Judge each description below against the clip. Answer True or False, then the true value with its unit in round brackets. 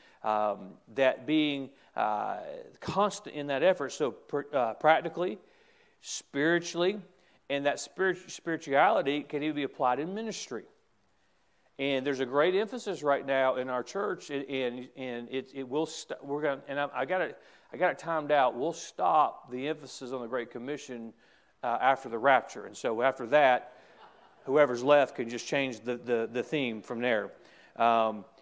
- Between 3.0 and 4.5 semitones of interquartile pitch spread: True (4.0 semitones)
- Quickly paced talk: False (165 wpm)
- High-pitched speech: False (140 Hz)